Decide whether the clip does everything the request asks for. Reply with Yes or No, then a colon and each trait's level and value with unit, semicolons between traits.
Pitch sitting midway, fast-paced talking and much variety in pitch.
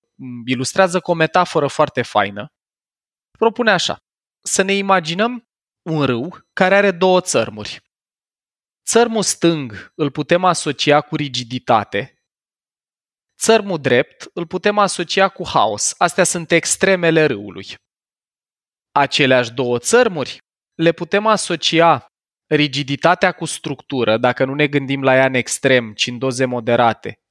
No: medium, 160 Hz; average, 125 wpm; wide, 6.0 semitones